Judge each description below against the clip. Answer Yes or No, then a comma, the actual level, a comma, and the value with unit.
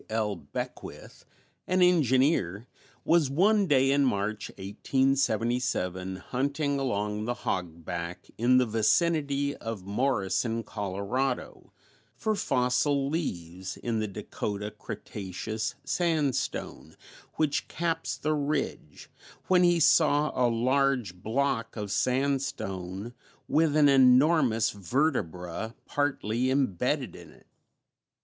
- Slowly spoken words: Yes, slow, 100 wpm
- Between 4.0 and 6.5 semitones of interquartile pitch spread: Yes, wide, 5.5 semitones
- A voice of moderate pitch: No, low, 125 Hz